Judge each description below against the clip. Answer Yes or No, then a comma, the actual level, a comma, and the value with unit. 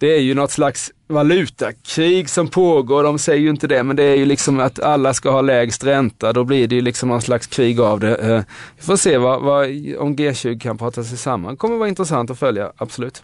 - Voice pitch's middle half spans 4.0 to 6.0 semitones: No, average, 3.4 semitones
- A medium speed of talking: No, fast, 230 wpm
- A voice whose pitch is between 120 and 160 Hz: Yes, low, 135 Hz